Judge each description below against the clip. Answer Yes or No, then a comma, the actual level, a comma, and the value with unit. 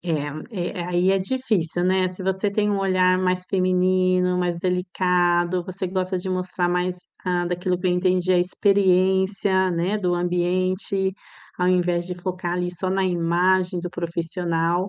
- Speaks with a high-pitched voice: No, medium, 180 Hz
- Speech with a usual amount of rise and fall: No, narrow, 1.0 semitones